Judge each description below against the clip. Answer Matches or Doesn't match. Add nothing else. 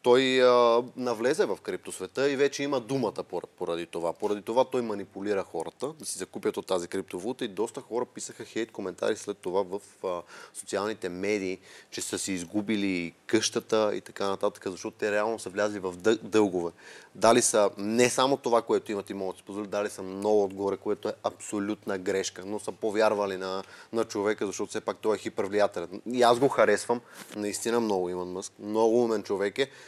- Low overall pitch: Matches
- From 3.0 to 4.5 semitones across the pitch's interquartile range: Matches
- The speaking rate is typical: Doesn't match